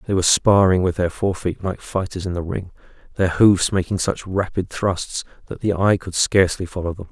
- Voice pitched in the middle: No, very low, 95 Hz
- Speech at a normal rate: No, fast, 210 wpm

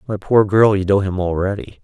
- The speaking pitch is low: Yes, low, 100 Hz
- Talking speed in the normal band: No, fast, 230 wpm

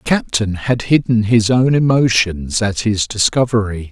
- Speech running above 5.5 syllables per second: No, 4.5 syllables/s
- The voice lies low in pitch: Yes, low, 110 Hz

